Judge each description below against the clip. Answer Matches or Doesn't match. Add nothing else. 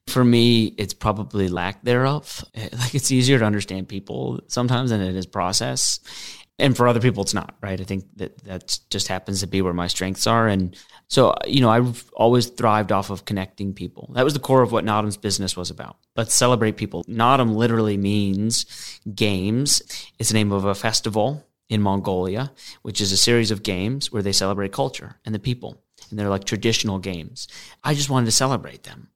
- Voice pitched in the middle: Doesn't match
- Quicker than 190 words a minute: Matches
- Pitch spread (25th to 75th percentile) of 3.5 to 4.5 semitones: Matches